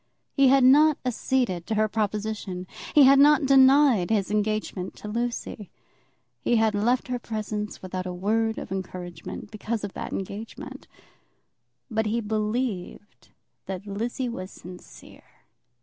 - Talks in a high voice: Yes, high, 215 Hz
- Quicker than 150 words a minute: No, slow, 135 wpm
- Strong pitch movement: No, average, 3.6 semitones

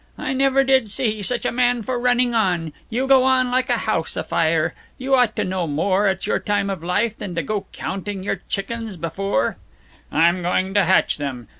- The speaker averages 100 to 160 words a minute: No, fast, 205 wpm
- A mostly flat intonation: No, wide, 5.5 semitones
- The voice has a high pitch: Yes, high, 205 Hz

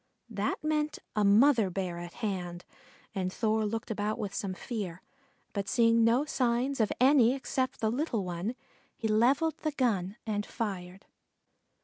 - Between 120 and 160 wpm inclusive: Yes, average, 150 wpm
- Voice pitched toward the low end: No, high, 220 Hz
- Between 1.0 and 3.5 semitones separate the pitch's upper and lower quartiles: No, average, 4.4 semitones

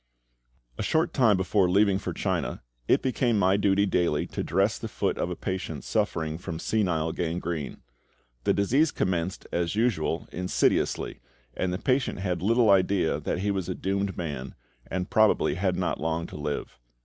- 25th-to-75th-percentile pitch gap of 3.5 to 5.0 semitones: No, average, 3.1 semitones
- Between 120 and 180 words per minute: Yes, average, 170 wpm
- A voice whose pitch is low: Yes, very low, 95 Hz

